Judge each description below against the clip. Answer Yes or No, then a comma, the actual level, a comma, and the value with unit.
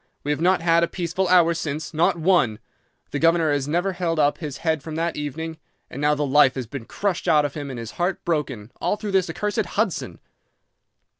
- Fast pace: Yes, fast, 210 wpm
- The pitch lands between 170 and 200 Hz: No, medium, 160 Hz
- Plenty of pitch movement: No, average, 3.1 semitones